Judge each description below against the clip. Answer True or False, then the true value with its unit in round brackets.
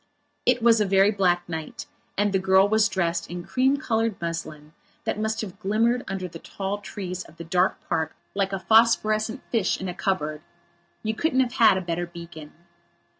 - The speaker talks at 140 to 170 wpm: False (185 wpm)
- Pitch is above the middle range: True (195 Hz)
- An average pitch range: True (4.0 semitones)